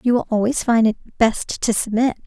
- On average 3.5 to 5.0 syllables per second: No, 5.5 syllables/s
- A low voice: No, high, 230 Hz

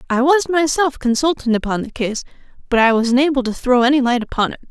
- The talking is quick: Yes, fast, 215 wpm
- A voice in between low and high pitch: No, very high, 260 Hz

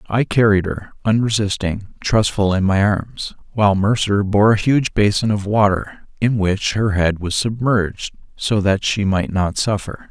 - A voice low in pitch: Yes, low, 105 Hz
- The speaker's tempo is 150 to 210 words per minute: Yes, average, 165 wpm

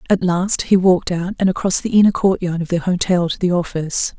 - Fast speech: Yes, fast, 230 wpm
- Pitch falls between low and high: Yes, medium, 180 Hz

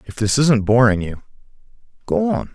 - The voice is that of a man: Yes, male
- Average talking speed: Yes, average, 165 wpm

